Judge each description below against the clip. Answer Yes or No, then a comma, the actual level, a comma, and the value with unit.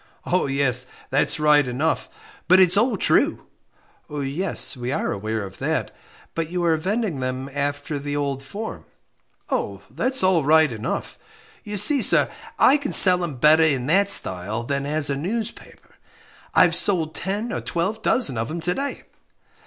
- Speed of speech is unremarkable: Yes, average, 160 wpm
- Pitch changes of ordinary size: No, wide, 5.7 semitones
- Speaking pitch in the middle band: Yes, medium, 155 Hz